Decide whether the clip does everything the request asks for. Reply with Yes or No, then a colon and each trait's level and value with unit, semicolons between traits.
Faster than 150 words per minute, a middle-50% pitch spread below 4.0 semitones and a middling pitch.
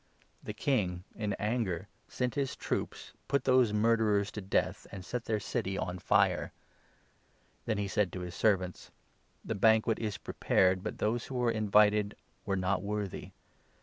No: average, 175 wpm; average, 2.9 semitones; low, 105 Hz